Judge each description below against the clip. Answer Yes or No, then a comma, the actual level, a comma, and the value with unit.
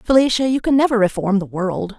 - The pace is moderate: No, fast, 210 wpm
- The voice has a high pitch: Yes, high, 220 Hz